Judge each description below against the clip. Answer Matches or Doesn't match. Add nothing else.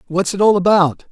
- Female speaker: Doesn't match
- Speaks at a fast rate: Matches